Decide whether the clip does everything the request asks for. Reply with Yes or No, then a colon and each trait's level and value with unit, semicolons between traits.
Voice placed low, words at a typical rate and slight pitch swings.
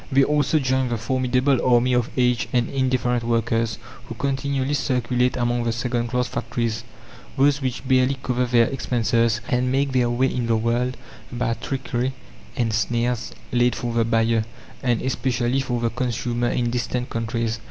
Yes: low, 125 Hz; average, 165 wpm; narrow, 1.7 semitones